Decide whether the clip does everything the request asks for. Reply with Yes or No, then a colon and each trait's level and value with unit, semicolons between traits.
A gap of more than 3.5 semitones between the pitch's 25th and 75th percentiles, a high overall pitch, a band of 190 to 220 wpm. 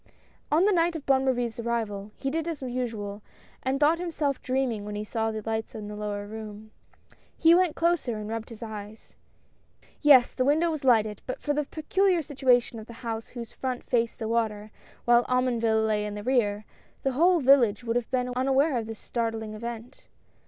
Yes: average, 3.9 semitones; high, 240 Hz; average, 200 wpm